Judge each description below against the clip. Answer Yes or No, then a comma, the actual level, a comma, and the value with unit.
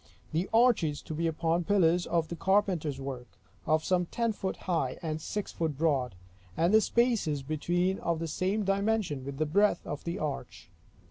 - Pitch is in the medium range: Yes, medium, 170 Hz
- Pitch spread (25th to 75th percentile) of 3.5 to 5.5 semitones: Yes, average, 4.2 semitones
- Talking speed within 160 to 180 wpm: Yes, average, 175 wpm